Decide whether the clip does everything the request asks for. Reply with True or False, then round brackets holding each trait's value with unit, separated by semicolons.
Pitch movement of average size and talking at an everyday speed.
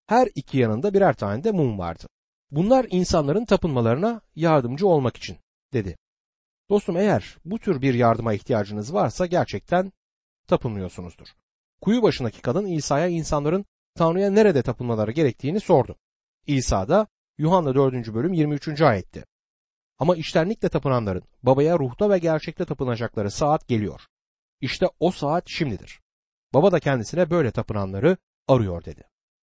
False (7.1 semitones; 130 wpm)